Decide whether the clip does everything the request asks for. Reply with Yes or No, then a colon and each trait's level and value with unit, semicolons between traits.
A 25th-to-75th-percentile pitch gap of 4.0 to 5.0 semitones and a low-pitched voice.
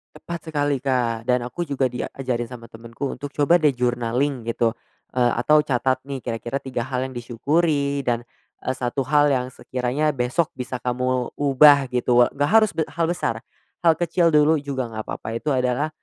No: average, 3.0 semitones; low, 130 Hz